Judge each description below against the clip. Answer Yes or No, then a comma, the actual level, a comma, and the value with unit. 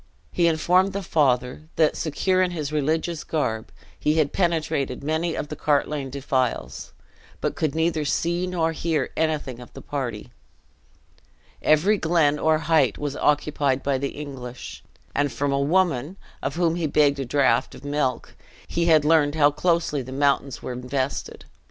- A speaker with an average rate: Yes, average, 160 wpm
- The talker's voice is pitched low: No, medium, 150 Hz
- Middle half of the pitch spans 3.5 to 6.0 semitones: No, average, 2.8 semitones